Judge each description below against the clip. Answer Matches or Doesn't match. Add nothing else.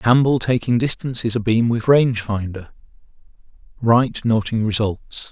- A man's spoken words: Matches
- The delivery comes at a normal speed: Doesn't match